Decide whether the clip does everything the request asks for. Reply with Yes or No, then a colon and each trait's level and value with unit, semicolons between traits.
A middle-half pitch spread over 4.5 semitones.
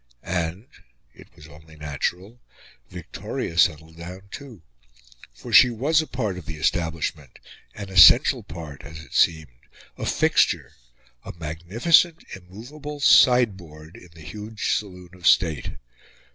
Yes: wide, 5.4 semitones